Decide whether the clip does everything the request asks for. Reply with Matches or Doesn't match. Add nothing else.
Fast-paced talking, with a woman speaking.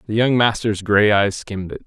Doesn't match